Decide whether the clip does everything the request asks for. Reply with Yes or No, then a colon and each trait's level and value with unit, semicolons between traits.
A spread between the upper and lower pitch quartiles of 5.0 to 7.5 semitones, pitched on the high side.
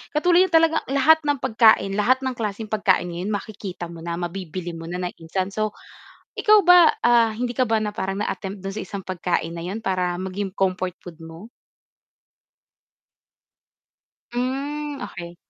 Yes: wide, 5.6 semitones; high, 200 Hz